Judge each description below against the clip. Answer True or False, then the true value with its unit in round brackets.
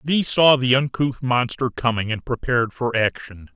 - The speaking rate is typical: True (170 wpm)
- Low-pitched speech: True (125 Hz)